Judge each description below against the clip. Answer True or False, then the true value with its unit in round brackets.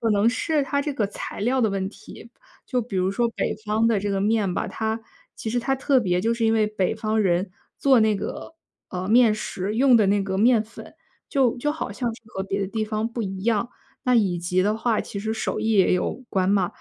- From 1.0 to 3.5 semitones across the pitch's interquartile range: True (3.0 semitones)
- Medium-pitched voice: False (215 Hz)